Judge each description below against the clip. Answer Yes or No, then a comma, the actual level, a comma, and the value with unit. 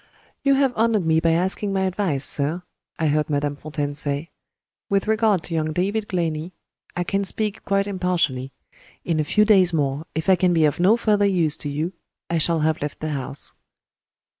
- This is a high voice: No, medium, 170 Hz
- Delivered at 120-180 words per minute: No, average, 190 wpm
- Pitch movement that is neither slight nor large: Yes, average, 4.5 semitones